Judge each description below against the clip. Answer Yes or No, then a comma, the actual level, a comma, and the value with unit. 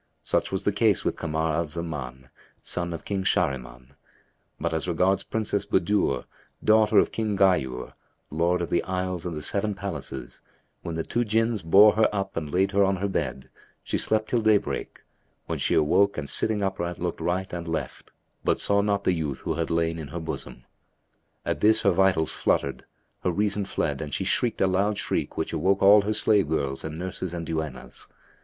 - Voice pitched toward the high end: No, very low, 90 Hz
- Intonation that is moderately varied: Yes, average, 4.0 semitones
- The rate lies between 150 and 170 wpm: No, average, 190 wpm